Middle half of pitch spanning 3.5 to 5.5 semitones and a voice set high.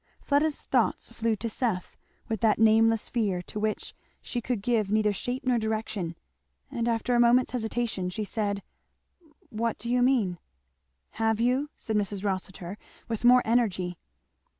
No: average, 2.8 semitones; high, 225 Hz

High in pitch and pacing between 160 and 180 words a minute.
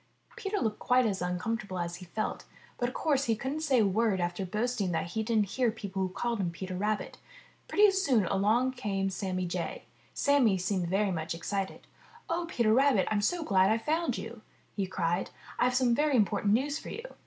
No: high, 215 Hz; average, 200 wpm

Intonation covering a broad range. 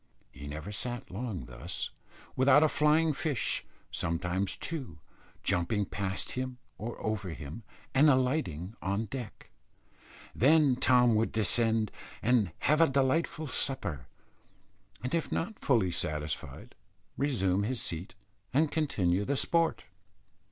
Yes: wide, 6.8 semitones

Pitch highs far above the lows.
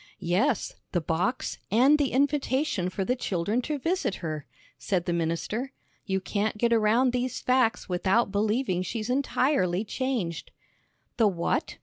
Yes: wide, 5.8 semitones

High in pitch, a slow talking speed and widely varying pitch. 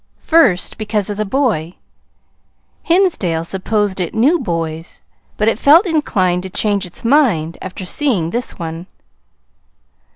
Yes: high, 205 Hz; slow, 130 wpm; wide, 6.5 semitones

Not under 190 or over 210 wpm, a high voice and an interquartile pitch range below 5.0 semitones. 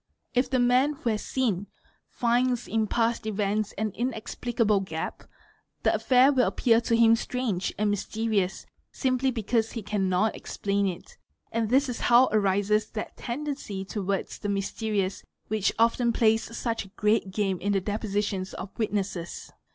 No: average, 160 wpm; high, 220 Hz; average, 3.0 semitones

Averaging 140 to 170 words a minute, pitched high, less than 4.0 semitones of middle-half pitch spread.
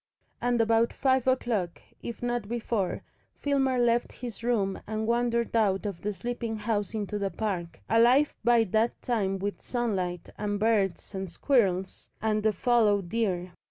Yes: average, 155 wpm; high, 220 Hz; average, 3.3 semitones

